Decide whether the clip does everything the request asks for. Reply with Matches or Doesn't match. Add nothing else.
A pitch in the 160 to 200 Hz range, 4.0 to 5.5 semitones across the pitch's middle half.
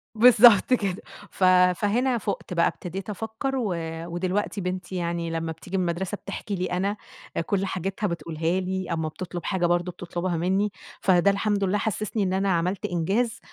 Doesn't match